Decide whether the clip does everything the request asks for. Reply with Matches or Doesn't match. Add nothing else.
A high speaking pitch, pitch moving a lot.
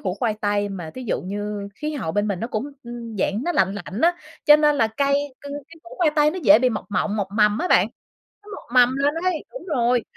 Matches